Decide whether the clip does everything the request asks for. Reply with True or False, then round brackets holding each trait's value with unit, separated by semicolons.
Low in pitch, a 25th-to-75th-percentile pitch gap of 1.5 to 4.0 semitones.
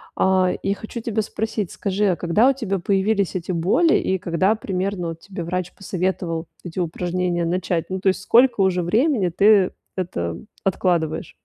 False (185 Hz; 2.6 semitones)